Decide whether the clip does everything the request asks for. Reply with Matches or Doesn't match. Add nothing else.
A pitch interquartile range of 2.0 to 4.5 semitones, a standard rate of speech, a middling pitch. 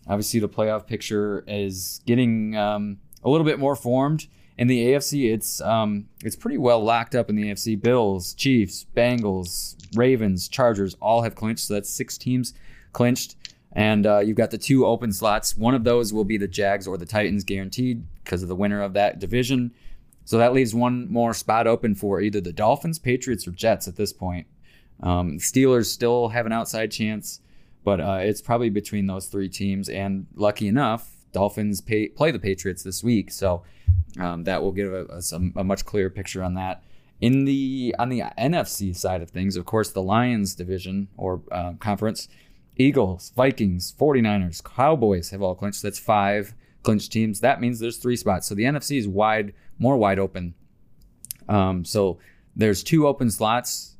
Doesn't match